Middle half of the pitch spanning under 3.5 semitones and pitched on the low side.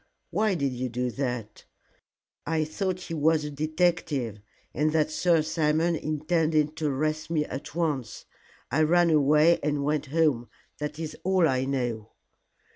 No: average, 2.7 semitones; medium, 155 Hz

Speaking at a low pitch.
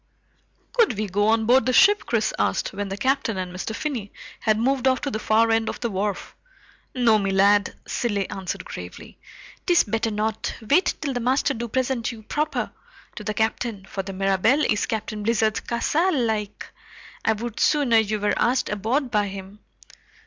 No: high, 220 Hz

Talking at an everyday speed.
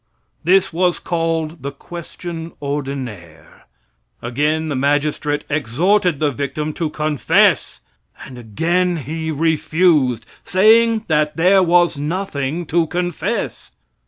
No: slow, 105 wpm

